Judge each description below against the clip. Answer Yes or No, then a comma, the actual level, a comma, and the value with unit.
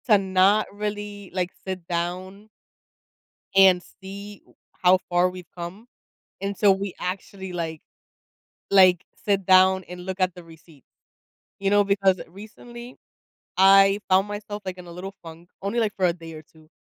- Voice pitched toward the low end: No, high, 190 Hz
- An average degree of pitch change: No, narrow, 2.0 semitones